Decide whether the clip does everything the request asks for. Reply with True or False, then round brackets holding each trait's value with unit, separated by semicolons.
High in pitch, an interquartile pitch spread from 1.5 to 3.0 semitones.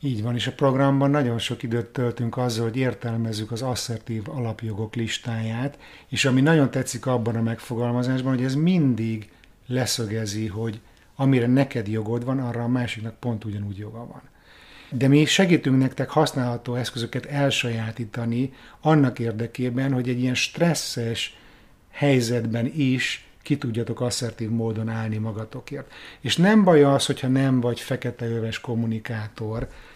False (120 Hz; 2.6 semitones)